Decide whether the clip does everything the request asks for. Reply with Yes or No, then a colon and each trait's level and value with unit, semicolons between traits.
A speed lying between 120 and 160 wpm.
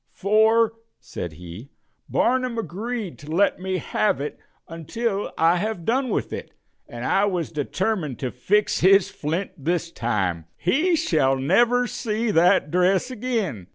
Yes: average, 145 wpm